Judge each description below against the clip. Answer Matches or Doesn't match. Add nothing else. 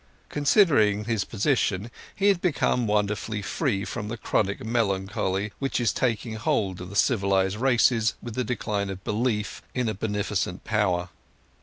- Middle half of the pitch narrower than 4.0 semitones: Matches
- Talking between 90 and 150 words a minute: Matches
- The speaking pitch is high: Doesn't match